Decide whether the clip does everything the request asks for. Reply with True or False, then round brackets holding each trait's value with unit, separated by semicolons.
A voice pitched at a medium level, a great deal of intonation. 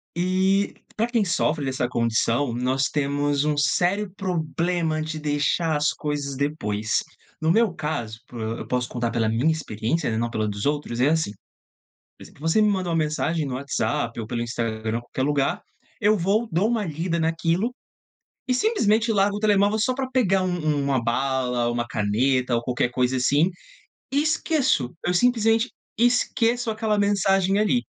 True (155 Hz; 8.1 semitones)